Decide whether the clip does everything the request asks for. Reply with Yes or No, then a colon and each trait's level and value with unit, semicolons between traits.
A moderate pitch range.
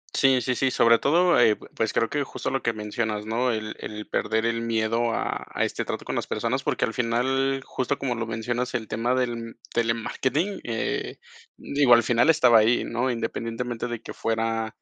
No: narrow, 2.1 semitones